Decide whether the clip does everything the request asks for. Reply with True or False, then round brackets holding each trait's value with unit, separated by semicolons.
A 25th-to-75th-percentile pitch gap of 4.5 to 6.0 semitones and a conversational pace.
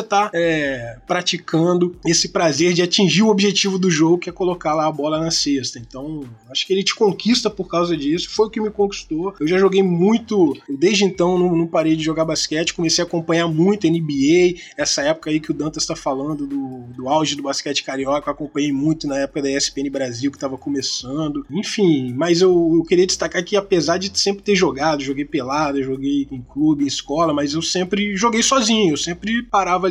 False (5.1 semitones; 205 wpm)